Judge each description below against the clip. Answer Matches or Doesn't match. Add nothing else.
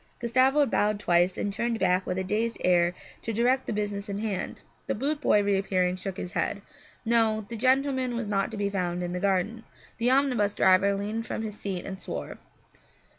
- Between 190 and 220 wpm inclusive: Matches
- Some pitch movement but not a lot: Matches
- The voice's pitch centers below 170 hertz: Doesn't match